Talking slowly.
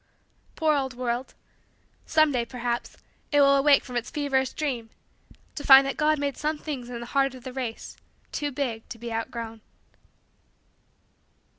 No: average, 155 wpm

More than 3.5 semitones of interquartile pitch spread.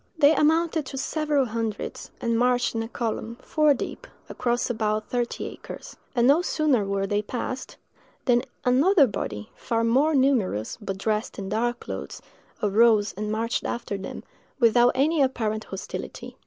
Yes: average, 4.1 semitones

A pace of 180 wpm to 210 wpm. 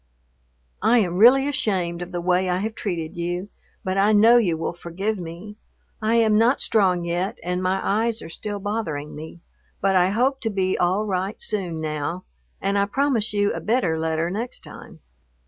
Yes: average, 185 wpm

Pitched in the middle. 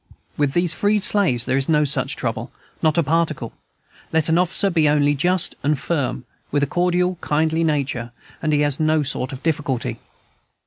Yes: medium, 155 Hz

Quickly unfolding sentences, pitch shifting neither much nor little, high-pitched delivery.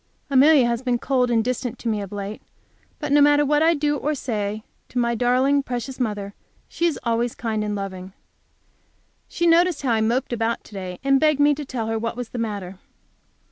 Yes: fast, 210 wpm; average, 4.5 semitones; high, 245 Hz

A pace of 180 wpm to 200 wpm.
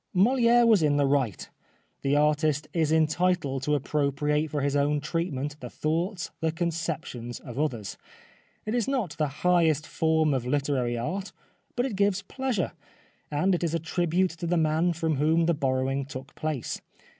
No: average, 165 wpm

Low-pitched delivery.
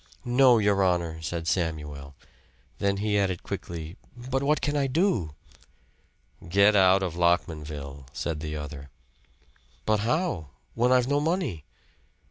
Yes: very low, 95 Hz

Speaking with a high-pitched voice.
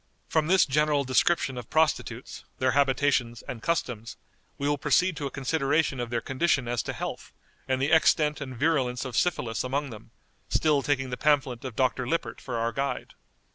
No: low, 135 Hz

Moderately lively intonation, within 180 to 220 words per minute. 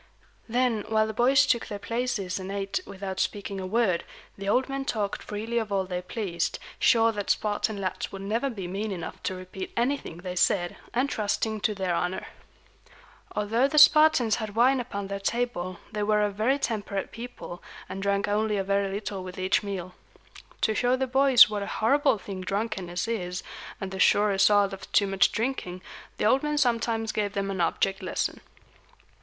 Yes: average, 3.2 semitones; average, 185 wpm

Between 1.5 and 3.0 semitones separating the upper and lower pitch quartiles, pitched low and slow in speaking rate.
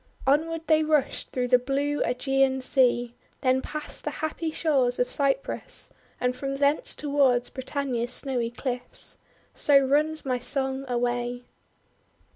No: narrow, 2.6 semitones; very high, 270 Hz; slow, 130 wpm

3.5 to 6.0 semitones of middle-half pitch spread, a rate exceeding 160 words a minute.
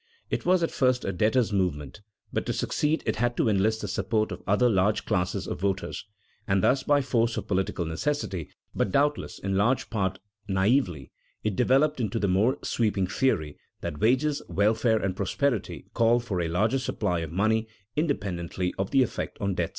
Yes: average, 5.0 semitones; average, 180 wpm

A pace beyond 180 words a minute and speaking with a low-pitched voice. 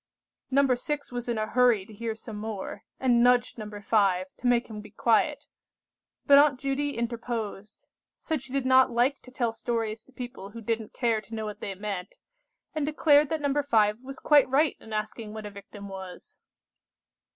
No: average, 190 wpm; high, 235 Hz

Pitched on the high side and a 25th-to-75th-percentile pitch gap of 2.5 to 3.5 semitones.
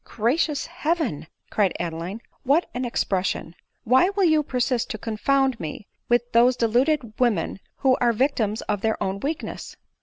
No: high, 240 Hz; average, 4.7 semitones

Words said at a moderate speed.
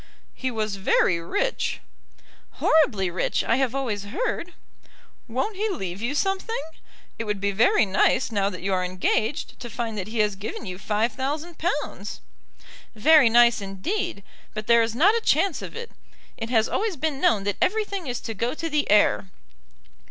Yes: average, 175 wpm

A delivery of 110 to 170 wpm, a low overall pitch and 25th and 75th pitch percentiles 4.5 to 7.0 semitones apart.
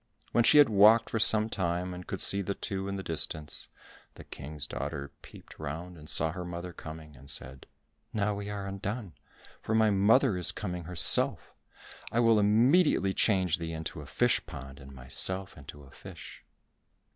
No: average, 180 wpm; very low, 90 Hz; average, 5.0 semitones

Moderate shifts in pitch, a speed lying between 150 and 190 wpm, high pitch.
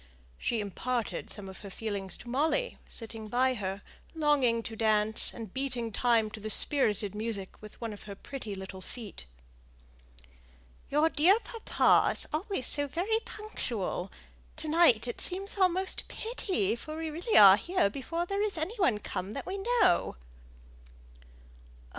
No: wide, 8.2 semitones; average, 155 wpm; high, 245 Hz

